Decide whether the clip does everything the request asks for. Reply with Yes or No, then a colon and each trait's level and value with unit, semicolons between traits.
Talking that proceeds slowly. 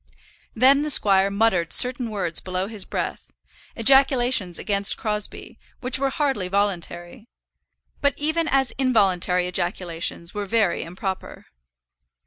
Yes: slow, 115 wpm